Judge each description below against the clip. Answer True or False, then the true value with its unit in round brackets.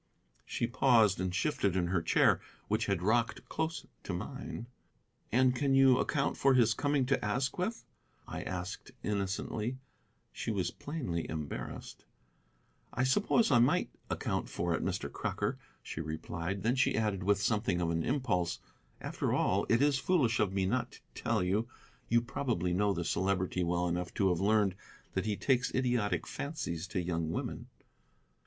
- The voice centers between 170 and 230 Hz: False (105 Hz)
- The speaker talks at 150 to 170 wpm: True (160 wpm)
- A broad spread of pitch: True (6.0 semitones)